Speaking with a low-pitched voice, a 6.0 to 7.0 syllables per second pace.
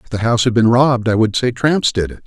Yes: low, 120 Hz; 6.5 syllables/s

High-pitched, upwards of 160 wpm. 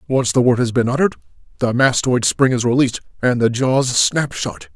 No: low, 120 Hz; average, 200 wpm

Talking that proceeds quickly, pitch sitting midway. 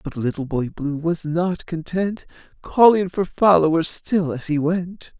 No: average, 160 wpm; medium, 165 Hz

